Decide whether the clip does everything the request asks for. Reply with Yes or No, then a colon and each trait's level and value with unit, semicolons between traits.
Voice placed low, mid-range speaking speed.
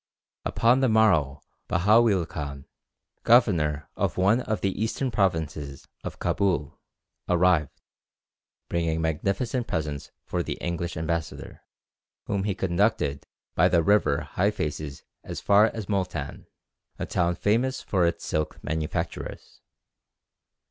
No: very low, 90 Hz; slow, 115 wpm